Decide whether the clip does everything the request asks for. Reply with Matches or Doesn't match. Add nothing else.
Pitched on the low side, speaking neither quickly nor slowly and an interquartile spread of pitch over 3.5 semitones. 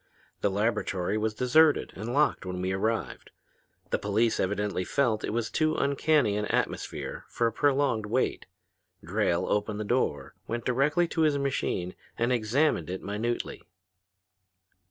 Matches